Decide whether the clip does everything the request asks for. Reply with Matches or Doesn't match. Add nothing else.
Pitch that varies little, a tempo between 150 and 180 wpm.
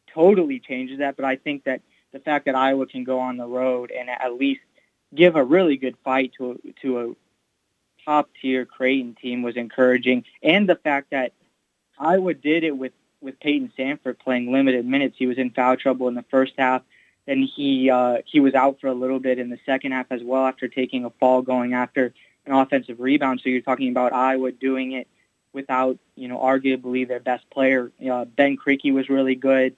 Doesn't match